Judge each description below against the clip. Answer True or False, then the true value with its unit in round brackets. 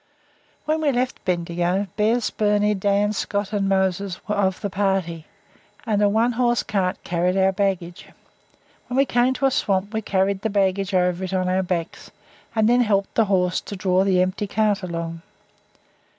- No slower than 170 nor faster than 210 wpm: True (180 wpm)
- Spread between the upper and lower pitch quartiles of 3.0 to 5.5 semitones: False (2.5 semitones)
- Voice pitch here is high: True (195 Hz)